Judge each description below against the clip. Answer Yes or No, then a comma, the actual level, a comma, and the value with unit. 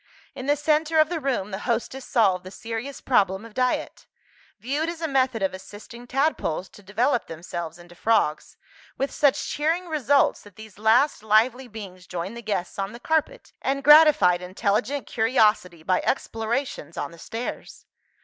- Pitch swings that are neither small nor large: No, wide, 6.3 semitones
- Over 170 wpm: No, average, 165 wpm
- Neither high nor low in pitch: No, high, 230 Hz